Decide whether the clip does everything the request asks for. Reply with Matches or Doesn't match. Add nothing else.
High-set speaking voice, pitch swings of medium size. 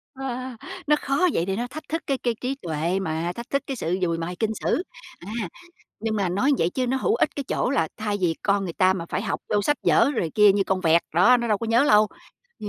Doesn't match